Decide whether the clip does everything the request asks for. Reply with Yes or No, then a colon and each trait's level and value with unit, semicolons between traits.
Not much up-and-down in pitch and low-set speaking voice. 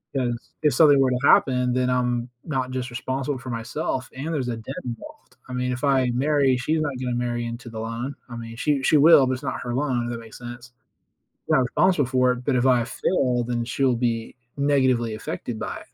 Yes: narrow, 2.0 semitones; low, 125 Hz